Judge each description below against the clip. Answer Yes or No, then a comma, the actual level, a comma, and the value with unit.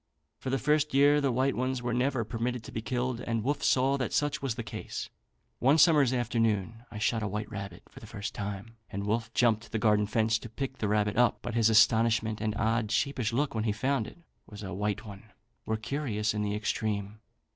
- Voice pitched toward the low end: Yes, low, 115 Hz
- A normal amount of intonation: Yes, average, 3.3 semitones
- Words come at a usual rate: No, fast, 220 wpm